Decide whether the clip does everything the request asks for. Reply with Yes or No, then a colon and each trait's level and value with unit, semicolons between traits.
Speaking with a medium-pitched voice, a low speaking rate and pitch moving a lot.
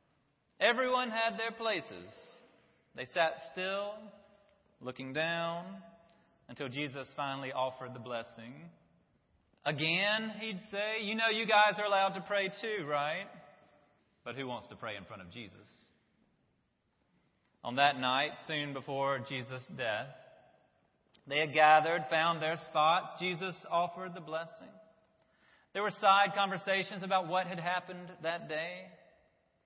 Yes: medium, 170 Hz; slow, 130 wpm; wide, 6.0 semitones